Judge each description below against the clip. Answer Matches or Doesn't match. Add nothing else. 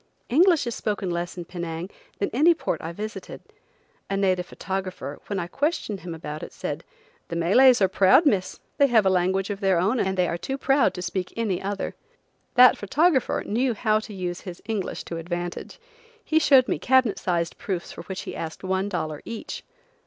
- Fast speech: Doesn't match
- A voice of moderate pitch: Doesn't match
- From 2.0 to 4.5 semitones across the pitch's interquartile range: Doesn't match